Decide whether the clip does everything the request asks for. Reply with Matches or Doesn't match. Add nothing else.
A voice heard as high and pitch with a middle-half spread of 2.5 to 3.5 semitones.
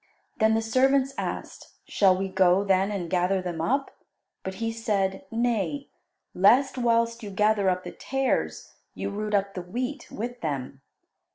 Doesn't match